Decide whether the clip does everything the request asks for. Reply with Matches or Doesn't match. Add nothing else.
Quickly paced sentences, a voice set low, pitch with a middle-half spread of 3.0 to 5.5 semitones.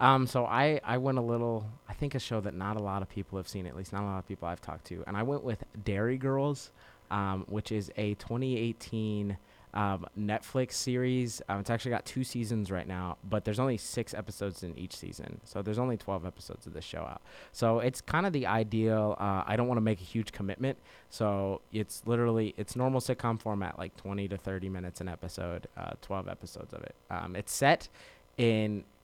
Matches